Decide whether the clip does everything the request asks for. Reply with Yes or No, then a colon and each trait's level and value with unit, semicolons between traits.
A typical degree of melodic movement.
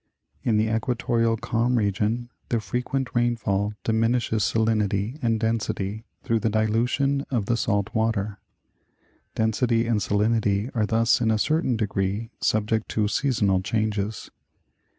No: narrow, 2.0 semitones